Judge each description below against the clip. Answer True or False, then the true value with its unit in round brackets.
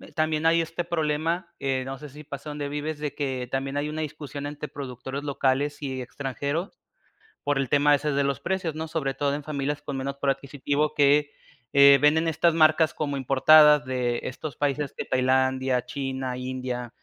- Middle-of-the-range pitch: True (145 Hz)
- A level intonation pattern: True (2.2 semitones)